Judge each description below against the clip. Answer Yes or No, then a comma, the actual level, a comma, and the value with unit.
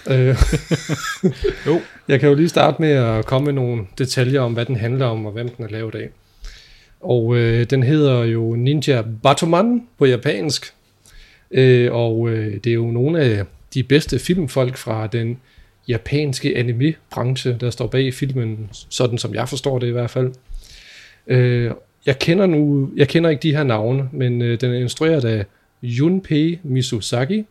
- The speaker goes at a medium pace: Yes, average, 170 wpm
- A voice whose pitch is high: No, low, 130 Hz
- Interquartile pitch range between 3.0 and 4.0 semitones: Yes, average, 3.5 semitones